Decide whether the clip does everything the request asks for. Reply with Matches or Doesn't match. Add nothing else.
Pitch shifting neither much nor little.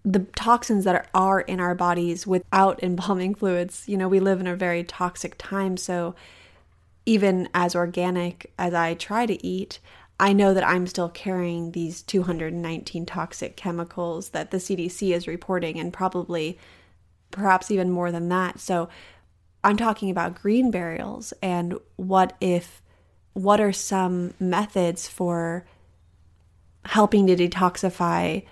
Doesn't match